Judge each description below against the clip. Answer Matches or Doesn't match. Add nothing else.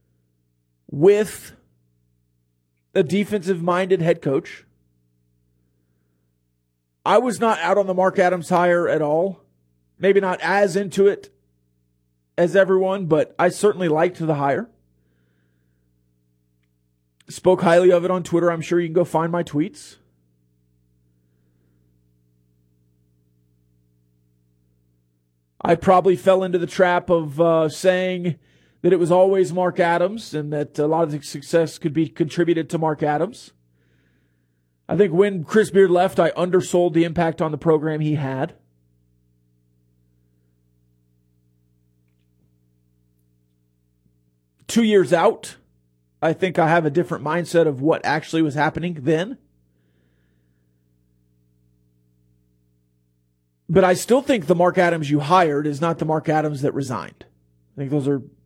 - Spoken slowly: Matches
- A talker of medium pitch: Doesn't match